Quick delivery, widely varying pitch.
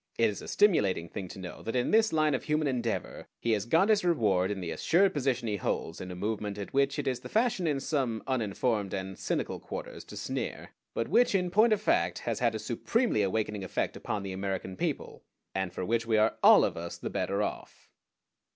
Yes: fast, 225 wpm; wide, 7.8 semitones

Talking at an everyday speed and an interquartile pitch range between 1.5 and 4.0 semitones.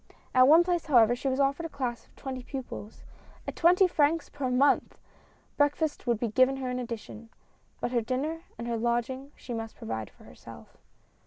Yes: average, 185 wpm; average, 3.4 semitones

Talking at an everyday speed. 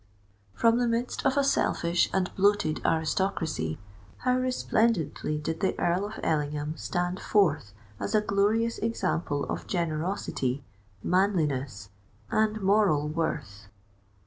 No: slow, 120 wpm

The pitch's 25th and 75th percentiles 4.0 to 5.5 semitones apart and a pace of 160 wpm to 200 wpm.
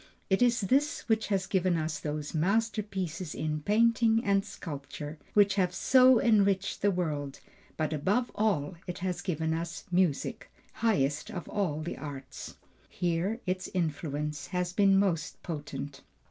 No: average, 4.9 semitones; average, 145 wpm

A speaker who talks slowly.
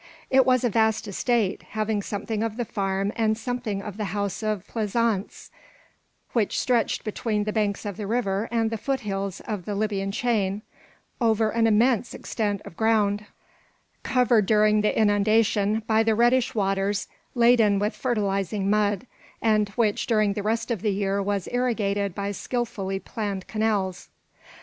No: average, 155 wpm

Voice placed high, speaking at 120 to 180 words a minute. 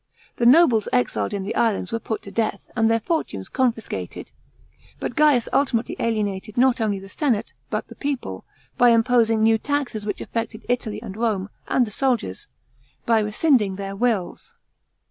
Yes: high, 225 Hz; average, 165 wpm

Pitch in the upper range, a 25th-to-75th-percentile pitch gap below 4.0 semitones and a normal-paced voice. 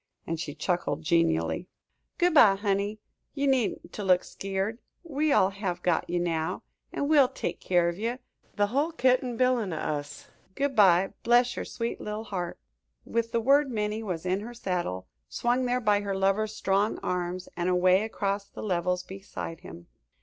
No: high, 200 Hz; average, 4.8 semitones; average, 180 wpm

